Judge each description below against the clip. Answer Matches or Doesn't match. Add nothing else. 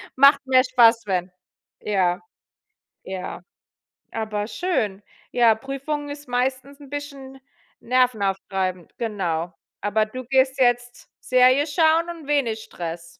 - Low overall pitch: Doesn't match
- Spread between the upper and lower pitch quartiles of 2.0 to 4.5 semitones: Doesn't match